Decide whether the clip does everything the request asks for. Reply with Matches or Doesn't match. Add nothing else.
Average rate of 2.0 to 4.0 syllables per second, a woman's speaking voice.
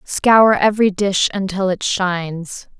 Matches